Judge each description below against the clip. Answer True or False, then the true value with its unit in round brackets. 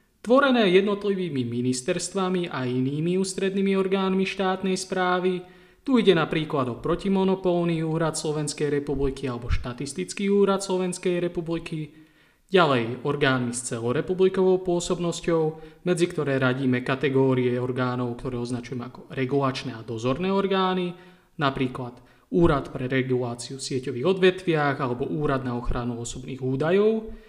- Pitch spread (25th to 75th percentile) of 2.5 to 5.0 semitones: False (6.1 semitones)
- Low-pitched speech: False (155 Hz)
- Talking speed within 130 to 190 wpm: False (115 wpm)